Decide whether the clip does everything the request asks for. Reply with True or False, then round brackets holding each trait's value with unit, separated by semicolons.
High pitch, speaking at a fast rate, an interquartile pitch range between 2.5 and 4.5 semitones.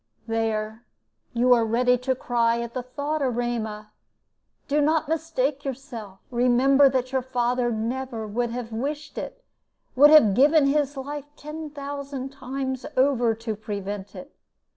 False (255 Hz; 140 wpm; 3.3 semitones)